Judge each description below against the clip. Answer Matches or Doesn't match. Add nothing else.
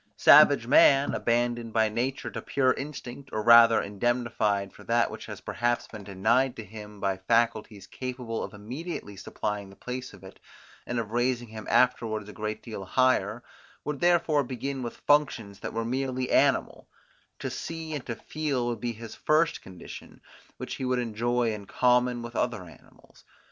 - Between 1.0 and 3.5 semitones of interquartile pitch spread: Matches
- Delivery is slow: Doesn't match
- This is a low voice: Matches